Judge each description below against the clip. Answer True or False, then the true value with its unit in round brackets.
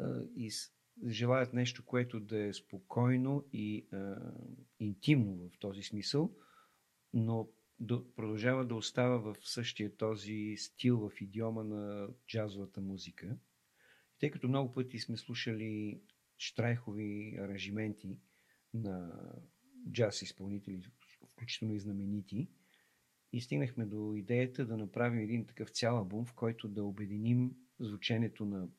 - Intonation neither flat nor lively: True (3.2 semitones)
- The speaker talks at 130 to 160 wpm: False (120 wpm)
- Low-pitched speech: True (110 Hz)